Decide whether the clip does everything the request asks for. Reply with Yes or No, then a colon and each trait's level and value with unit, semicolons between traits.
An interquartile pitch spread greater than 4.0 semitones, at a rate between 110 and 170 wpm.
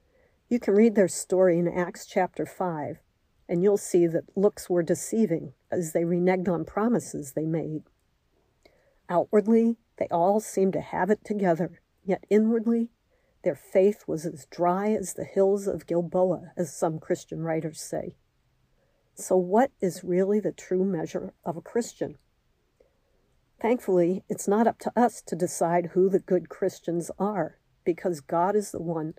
No: average, 3.3 semitones; average, 155 wpm